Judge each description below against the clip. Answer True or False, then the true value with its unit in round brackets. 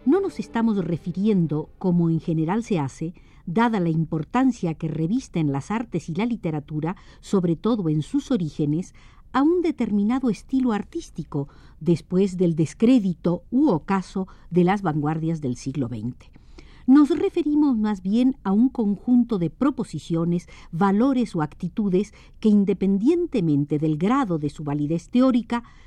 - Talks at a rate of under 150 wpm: True (140 wpm)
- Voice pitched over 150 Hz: True (190 Hz)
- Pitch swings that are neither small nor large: False (6.6 semitones)